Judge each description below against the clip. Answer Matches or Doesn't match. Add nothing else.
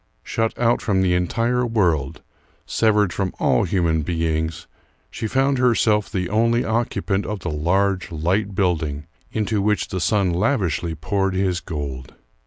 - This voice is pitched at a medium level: Doesn't match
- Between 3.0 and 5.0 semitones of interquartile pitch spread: Matches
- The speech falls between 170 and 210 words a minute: Doesn't match